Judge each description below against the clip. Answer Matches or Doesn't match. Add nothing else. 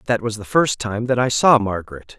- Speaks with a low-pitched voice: Matches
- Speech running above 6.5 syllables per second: Doesn't match